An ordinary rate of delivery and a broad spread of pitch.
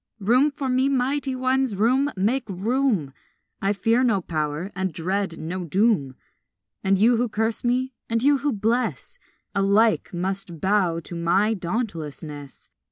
Yes: average, 145 wpm; wide, 5.7 semitones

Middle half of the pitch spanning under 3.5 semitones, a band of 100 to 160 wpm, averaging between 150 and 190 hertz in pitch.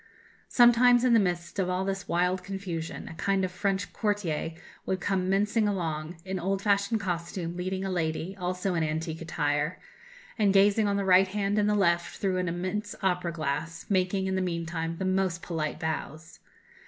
No: average, 2.8 semitones; average, 180 wpm; medium, 185 Hz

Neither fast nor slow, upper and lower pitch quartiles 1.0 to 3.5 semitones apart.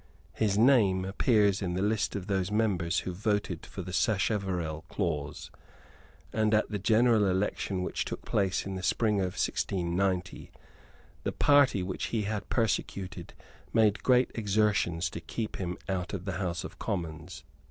Yes: average, 155 wpm; average, 2.9 semitones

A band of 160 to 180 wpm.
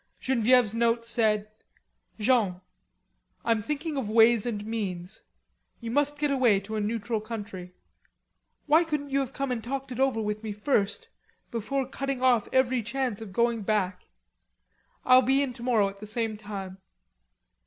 No: average, 150 wpm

